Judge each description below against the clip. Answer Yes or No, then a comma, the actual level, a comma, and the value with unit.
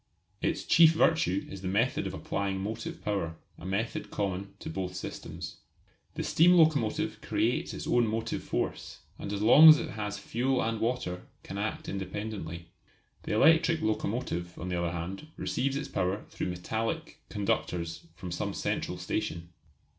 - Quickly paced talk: No, average, 160 wpm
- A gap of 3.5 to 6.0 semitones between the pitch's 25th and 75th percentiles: Yes, average, 4.6 semitones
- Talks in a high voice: No, low, 105 Hz